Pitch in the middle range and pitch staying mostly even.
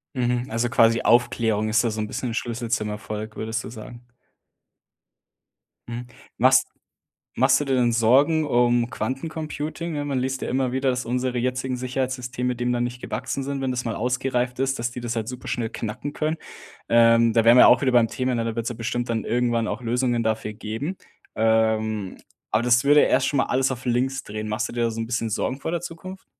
No: low, 120 Hz; narrow, 2.2 semitones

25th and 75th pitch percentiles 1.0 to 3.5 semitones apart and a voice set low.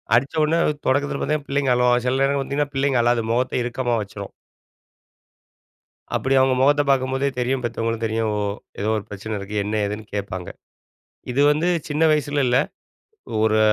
No: average, 4.0 semitones; low, 125 Hz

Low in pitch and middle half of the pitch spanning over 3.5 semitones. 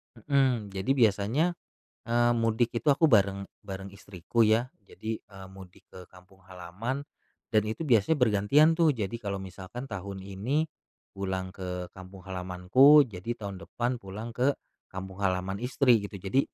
Yes: low, 100 Hz; average, 4.2 semitones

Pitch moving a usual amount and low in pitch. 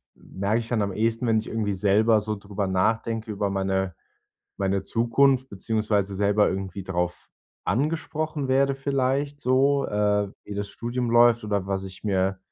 Yes: average, 3.6 semitones; low, 105 Hz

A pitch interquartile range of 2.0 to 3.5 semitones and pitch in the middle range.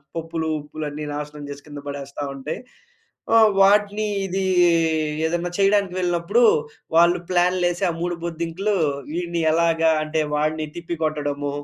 Yes: average, 2.9 semitones; medium, 170 Hz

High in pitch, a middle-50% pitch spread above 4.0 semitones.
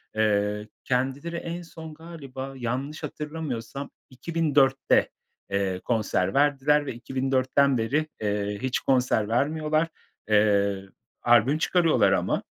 No: low, 135 Hz; average, 5.2 semitones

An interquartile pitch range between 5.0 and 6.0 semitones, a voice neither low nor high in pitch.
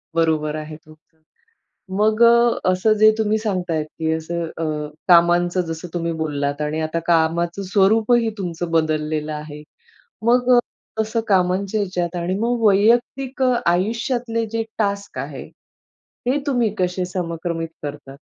Yes: wide, 5.4 semitones; medium, 180 Hz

